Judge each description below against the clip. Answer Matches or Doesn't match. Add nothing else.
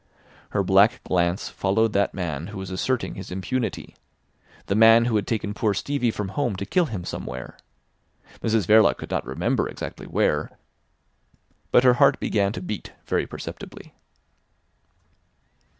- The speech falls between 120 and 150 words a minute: Matches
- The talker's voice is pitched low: Matches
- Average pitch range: Matches